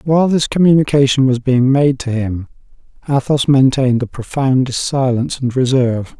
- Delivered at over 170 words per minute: No, average, 145 wpm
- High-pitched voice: No, low, 130 Hz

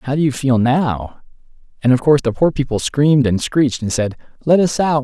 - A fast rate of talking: Yes, fast, 225 wpm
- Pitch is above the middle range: No, low, 135 Hz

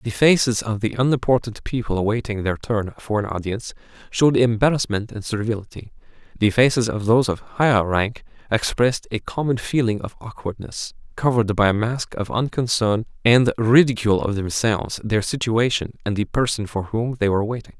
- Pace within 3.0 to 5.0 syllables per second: No, 5.5 syllables/s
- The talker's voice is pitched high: No, low, 110 Hz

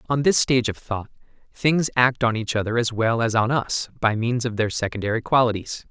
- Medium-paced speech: No, fast, 215 wpm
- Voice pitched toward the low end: Yes, low, 120 Hz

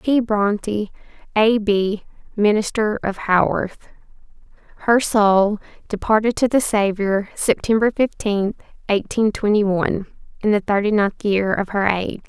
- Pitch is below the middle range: No, high, 210 Hz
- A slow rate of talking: Yes, slow, 125 wpm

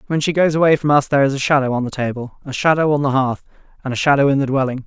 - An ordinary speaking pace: No, fast, 295 wpm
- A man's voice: Yes, male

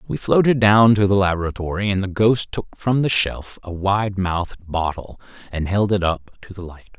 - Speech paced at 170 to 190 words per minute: No, fast, 205 wpm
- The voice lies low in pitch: Yes, low, 100 Hz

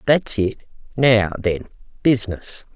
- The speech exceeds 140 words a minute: No, slow, 110 wpm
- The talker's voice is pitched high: No, low, 110 Hz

